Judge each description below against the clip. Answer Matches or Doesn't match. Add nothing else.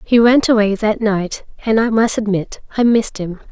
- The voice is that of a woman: Matches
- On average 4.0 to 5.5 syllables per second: Matches